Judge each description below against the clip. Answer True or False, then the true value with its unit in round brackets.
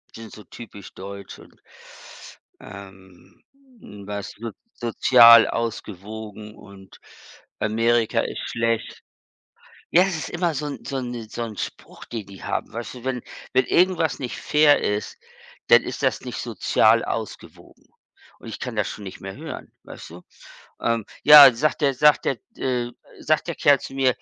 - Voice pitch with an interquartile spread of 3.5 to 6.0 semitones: True (4.3 semitones)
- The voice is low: True (115 Hz)